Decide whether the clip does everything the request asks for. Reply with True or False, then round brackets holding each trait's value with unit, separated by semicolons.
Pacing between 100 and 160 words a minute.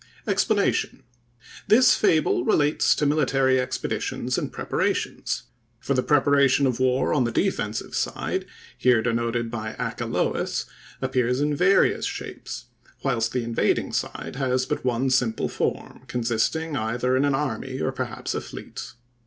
True (135 wpm)